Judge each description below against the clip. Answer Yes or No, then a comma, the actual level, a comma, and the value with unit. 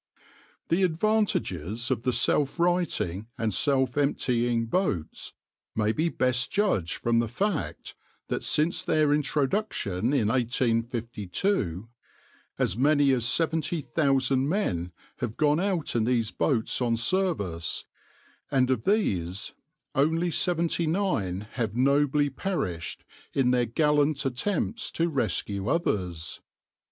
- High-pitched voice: No, low, 130 Hz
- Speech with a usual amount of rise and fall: No, wide, 6.4 semitones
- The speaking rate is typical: No, slow, 120 wpm